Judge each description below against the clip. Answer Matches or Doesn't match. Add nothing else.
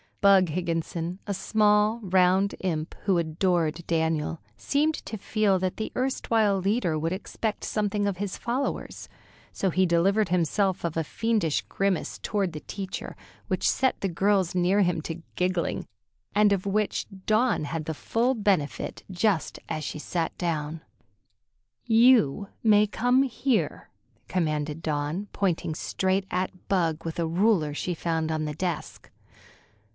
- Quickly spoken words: Doesn't match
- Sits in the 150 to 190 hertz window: Matches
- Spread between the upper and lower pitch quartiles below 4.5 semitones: Matches